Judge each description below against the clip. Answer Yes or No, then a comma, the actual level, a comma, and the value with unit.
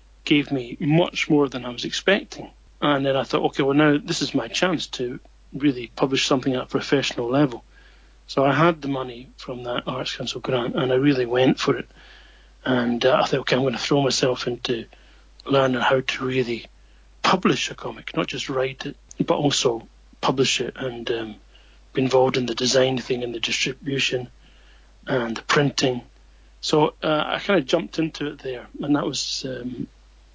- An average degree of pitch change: Yes, average, 3.0 semitones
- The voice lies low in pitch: Yes, low, 130 Hz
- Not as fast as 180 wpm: No, average, 190 wpm